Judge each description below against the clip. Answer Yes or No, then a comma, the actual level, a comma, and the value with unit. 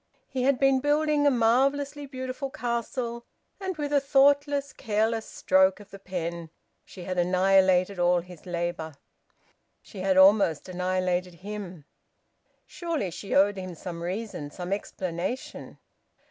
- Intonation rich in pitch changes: Yes, wide, 6.5 semitones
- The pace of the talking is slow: Yes, slow, 130 wpm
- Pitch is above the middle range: Yes, high, 200 Hz